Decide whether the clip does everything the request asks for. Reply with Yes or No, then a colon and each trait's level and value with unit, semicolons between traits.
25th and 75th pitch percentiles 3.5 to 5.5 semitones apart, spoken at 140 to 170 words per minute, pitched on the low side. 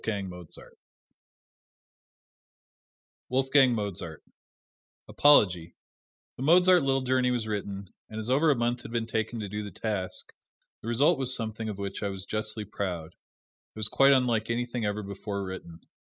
Yes: average, 4.1 semitones; average, 150 wpm; low, 110 Hz